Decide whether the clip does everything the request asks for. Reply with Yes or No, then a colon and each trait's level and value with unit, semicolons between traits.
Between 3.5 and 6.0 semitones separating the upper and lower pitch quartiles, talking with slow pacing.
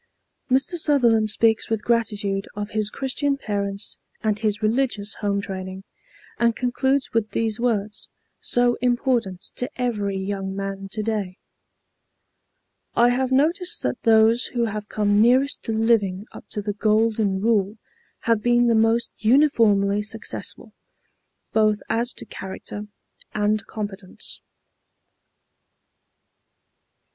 No: average, 2.9 semitones; slow, 120 wpm